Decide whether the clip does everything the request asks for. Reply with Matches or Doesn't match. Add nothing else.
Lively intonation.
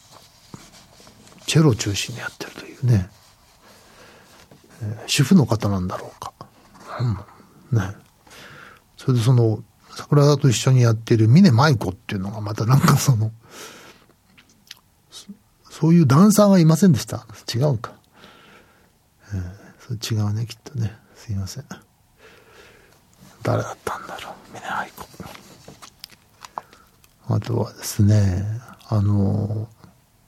Doesn't match